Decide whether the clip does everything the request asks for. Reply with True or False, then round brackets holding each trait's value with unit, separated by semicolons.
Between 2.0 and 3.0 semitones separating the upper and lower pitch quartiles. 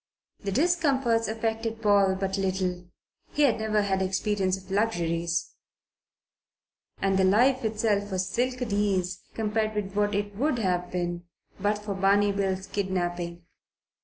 True (2.7 semitones)